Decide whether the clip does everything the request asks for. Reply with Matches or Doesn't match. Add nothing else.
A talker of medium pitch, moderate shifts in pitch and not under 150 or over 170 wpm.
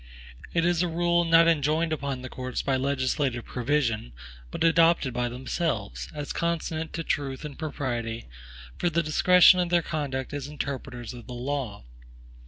Matches